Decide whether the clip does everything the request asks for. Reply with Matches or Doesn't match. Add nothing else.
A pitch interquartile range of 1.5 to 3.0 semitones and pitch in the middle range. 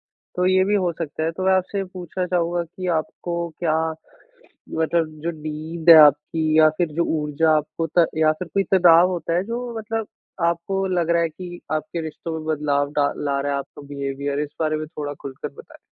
Matches